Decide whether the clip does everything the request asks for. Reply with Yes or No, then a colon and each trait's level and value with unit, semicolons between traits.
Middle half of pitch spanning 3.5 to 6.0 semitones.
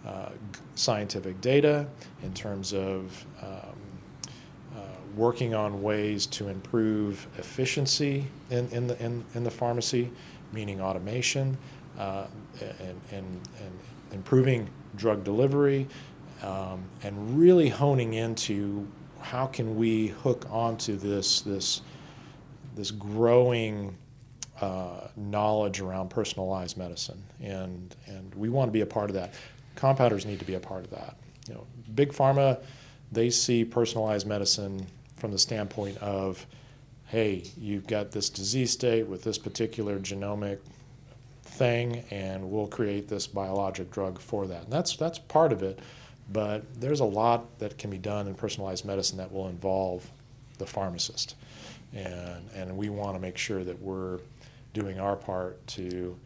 Yes: average, 4.5 semitones